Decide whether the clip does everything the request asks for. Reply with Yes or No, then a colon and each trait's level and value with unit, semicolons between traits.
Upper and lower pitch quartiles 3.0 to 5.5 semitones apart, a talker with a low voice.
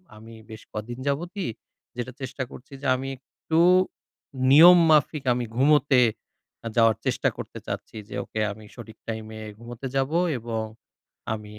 Yes: average, 4.1 semitones; low, 125 Hz